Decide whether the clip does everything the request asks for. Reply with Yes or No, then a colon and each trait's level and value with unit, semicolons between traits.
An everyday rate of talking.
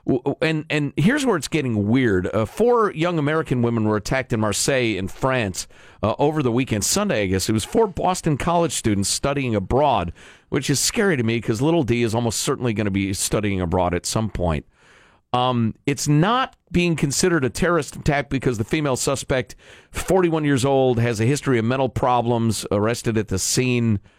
Yes: average, 190 wpm